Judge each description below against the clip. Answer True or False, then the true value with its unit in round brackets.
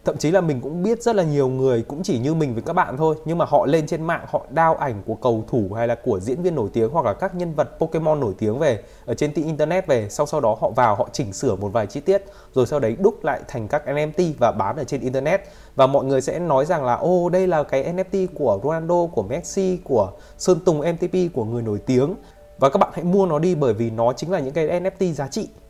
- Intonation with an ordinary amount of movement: False (5.8 semitones)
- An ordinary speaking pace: False (275 wpm)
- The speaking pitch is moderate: True (155 Hz)